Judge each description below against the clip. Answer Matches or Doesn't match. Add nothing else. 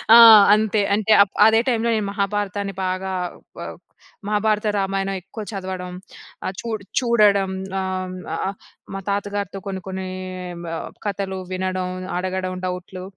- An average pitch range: Doesn't match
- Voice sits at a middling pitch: Doesn't match